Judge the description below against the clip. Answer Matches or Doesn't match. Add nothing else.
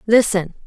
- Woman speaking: Matches